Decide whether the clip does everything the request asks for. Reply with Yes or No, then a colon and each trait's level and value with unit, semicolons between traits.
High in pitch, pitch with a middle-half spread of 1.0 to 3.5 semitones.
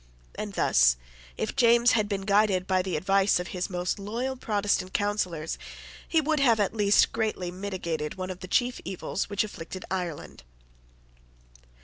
Yes: high, 195 Hz; average, 2.9 semitones